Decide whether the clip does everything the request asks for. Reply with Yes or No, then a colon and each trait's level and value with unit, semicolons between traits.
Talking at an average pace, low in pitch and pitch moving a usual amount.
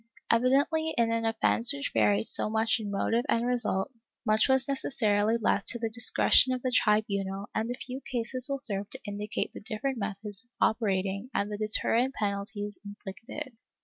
No: average, 180 wpm; high, 220 Hz; average, 3.4 semitones